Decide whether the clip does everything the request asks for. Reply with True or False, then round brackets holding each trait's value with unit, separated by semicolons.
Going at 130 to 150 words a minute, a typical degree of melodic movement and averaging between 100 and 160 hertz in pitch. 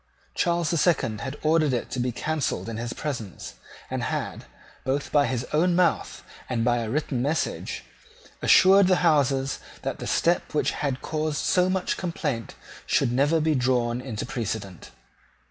False (165 wpm; 4.8 semitones; 140 Hz)